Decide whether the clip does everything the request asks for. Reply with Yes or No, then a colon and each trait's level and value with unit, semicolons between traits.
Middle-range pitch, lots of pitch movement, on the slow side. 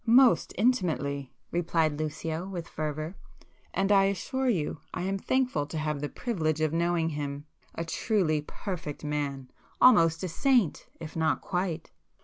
No: medium, 165 Hz; average, 4.2 semitones; slow, 130 wpm